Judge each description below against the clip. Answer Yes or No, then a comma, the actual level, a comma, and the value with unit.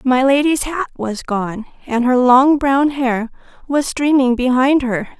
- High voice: Yes, very high, 260 Hz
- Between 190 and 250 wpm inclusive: No, average, 160 wpm